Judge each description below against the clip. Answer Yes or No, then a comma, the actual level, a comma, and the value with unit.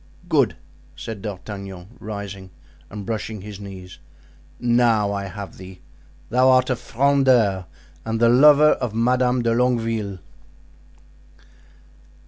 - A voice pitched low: Yes, low, 110 Hz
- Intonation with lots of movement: No, average, 3.8 semitones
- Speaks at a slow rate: Yes, slow, 110 wpm